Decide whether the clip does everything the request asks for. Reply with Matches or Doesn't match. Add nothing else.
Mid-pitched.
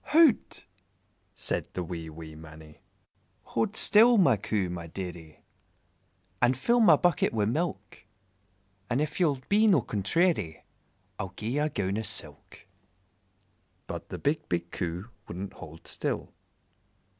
Doesn't match